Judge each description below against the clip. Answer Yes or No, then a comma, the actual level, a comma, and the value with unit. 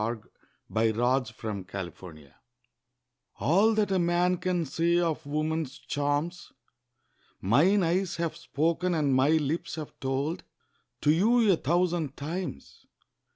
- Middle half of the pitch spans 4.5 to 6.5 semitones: Yes, average, 4.8 semitones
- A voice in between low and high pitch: Yes, medium, 160 Hz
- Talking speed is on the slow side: Yes, slow, 130 wpm